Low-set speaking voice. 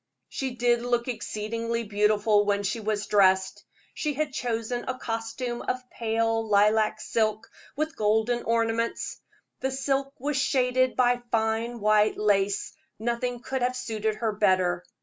No: high, 230 Hz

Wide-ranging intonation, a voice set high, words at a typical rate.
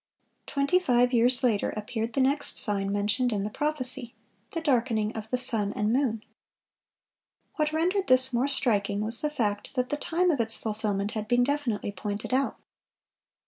No: average, 4.5 semitones; high, 240 Hz; average, 165 wpm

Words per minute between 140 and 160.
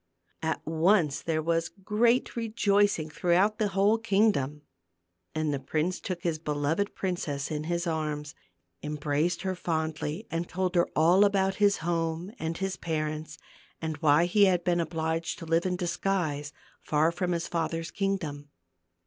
Yes: average, 150 wpm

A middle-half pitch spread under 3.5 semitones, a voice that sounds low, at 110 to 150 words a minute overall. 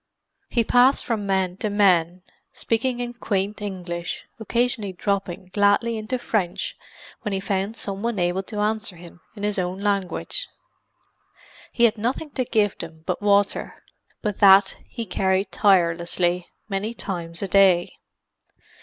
No: average, 3.0 semitones; high, 200 Hz; average, 145 wpm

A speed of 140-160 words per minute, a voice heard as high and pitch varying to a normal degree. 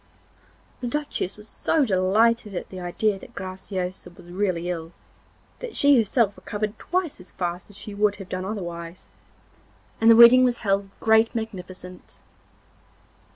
Yes: average, 155 wpm; high, 200 Hz; average, 3.8 semitones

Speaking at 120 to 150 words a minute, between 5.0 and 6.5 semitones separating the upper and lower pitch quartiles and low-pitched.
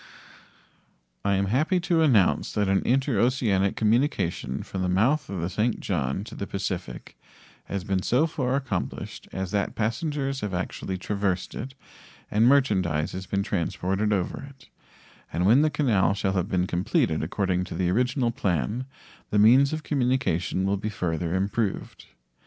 No: average, 160 wpm; wide, 5.4 semitones; low, 100 Hz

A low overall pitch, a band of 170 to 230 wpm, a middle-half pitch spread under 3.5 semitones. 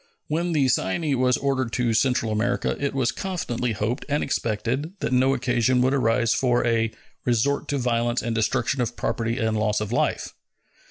Yes: low, 125 Hz; average, 175 wpm; average, 2.8 semitones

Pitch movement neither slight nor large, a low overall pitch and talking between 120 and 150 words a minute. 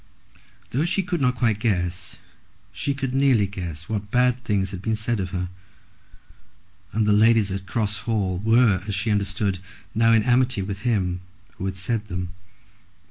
No: average, 3.5 semitones; low, 105 Hz; average, 170 wpm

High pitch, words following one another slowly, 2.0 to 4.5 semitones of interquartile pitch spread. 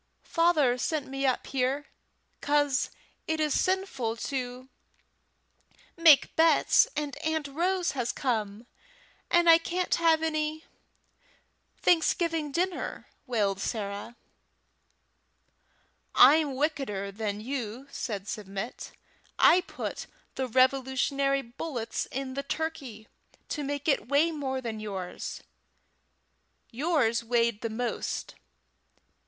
No: very high, 270 Hz; slow, 105 wpm; average, 5.1 semitones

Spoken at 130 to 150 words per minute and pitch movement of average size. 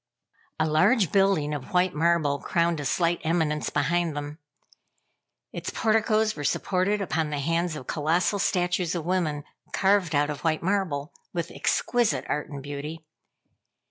Yes: average, 145 wpm; average, 3.6 semitones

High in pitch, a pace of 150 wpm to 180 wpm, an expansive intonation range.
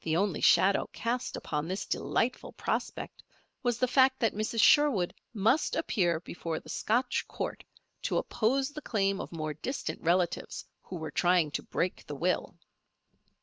Yes: high, 195 Hz; average, 155 wpm; wide, 6.2 semitones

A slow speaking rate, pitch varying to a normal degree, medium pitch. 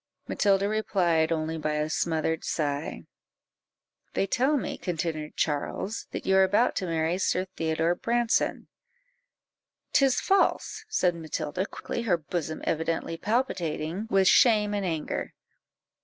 Yes: slow, 125 wpm; average, 4.4 semitones; medium, 175 Hz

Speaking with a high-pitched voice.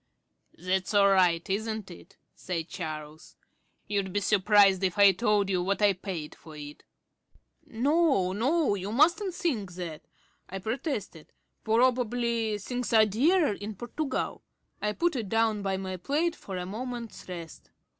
Yes: high, 205 Hz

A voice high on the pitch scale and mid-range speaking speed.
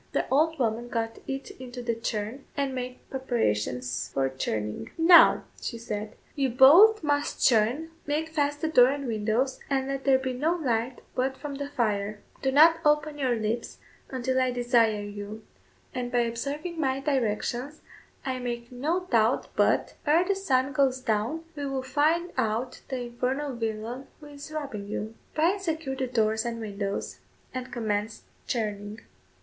Yes: very high, 255 Hz; average, 165 wpm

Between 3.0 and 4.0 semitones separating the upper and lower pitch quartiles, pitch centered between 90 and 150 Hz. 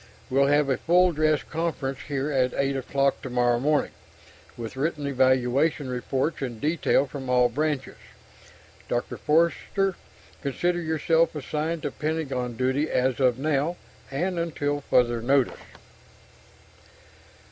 Yes: average, 3.3 semitones; medium, 140 Hz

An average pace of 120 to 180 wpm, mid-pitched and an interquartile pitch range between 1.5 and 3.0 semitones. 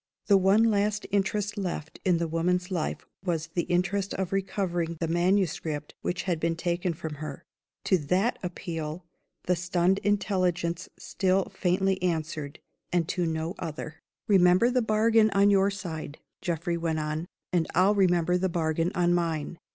Yes: average, 155 wpm; medium, 180 Hz; average, 2.7 semitones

